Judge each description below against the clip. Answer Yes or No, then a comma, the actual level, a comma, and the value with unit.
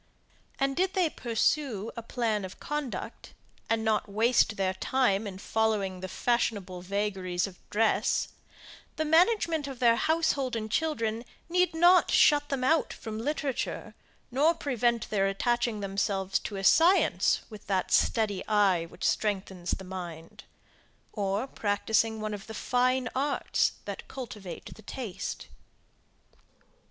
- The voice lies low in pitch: No, high, 220 Hz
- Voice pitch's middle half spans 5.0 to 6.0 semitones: Yes, average, 5.3 semitones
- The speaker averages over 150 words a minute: No, slow, 135 wpm